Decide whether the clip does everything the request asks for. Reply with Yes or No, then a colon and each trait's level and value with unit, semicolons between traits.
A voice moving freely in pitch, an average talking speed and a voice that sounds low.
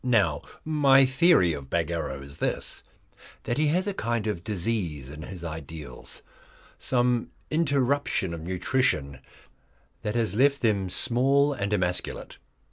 No: wide, 8.1 semitones; slow, 130 wpm; low, 105 Hz